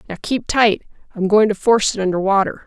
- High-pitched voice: Yes, high, 205 Hz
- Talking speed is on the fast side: Yes, fast, 225 wpm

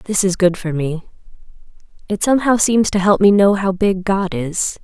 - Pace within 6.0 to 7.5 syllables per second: No, 4.7 syllables/s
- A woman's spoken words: Yes, female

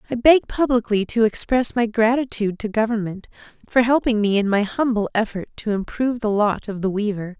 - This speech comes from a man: No, female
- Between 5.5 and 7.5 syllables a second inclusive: Yes, 5.6 syllables/s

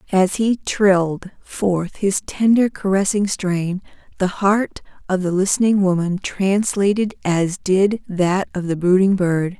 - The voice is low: No, high, 190 Hz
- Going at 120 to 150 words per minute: Yes, average, 140 wpm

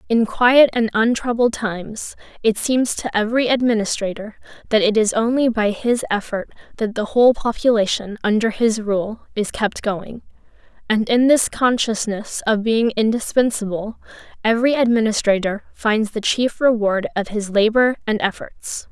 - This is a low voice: No, high, 220 Hz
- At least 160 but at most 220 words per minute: No, average, 145 wpm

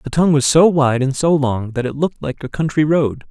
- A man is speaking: Yes, male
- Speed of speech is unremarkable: No, fast, 270 wpm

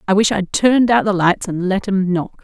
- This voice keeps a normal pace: No, fast, 270 wpm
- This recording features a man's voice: No, female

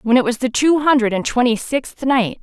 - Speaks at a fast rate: Yes, fast, 245 wpm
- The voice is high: Yes, very high, 250 Hz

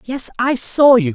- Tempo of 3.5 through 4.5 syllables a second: Yes, 3.9 syllables/s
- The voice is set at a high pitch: Yes, high, 245 Hz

